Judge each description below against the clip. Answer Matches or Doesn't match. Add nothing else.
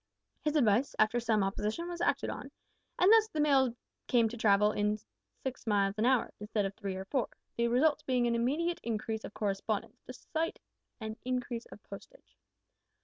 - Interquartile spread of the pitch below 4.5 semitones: Doesn't match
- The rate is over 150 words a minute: Matches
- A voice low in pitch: Doesn't match